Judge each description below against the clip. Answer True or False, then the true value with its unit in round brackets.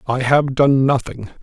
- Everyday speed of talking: True (170 wpm)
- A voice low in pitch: True (130 Hz)